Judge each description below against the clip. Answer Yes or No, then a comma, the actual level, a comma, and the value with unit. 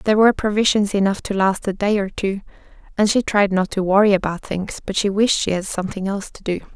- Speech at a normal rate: No, fast, 240 wpm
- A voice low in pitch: No, high, 200 Hz